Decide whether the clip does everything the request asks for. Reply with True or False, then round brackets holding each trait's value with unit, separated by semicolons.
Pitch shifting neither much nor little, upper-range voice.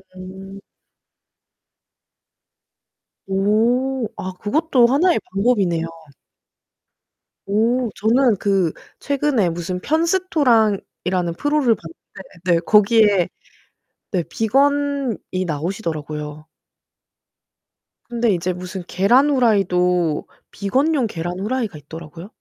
False (6.0 semitones; 205 Hz)